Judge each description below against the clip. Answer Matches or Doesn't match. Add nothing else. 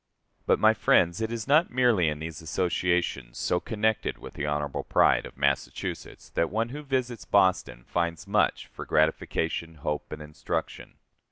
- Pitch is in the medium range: Doesn't match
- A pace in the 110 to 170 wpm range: Matches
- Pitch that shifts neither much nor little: Doesn't match